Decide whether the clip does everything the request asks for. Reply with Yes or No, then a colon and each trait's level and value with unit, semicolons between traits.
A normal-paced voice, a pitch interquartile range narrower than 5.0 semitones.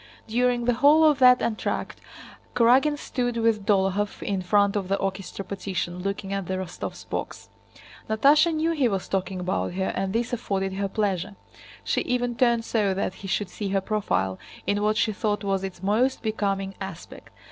Yes: average, 180 wpm; average, 3.6 semitones